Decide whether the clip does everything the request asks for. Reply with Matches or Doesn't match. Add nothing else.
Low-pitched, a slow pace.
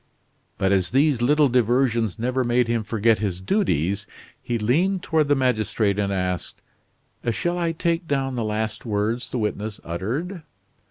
Doesn't match